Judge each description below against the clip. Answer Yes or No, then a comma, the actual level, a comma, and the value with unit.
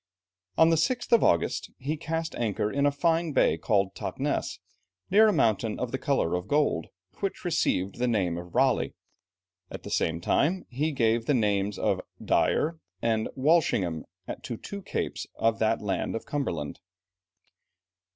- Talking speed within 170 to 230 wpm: No, average, 160 wpm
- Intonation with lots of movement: Yes, wide, 7.7 semitones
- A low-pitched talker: Yes, low, 120 Hz